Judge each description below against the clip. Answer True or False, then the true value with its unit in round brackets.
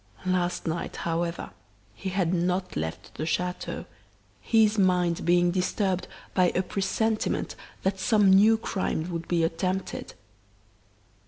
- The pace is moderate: False (120 wpm)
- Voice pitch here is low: False (180 Hz)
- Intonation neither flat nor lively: False (2.0 semitones)